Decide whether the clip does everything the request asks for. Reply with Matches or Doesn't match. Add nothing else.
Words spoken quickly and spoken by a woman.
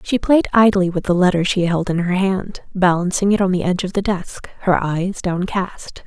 Matches